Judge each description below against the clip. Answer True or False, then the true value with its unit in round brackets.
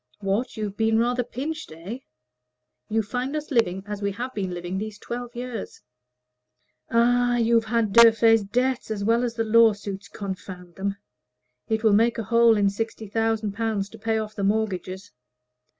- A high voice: True (220 Hz)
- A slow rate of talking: False (165 wpm)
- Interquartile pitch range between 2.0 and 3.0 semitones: True (2.6 semitones)